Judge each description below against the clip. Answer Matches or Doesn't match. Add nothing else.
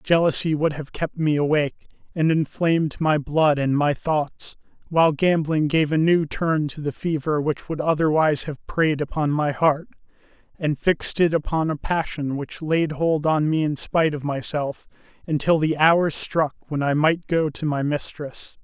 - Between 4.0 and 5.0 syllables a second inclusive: Matches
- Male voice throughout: Matches